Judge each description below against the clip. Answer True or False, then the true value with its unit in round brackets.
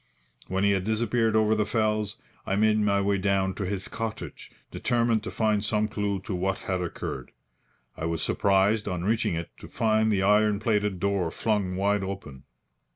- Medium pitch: False (100 Hz)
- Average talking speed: True (180 wpm)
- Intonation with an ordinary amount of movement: False (2.0 semitones)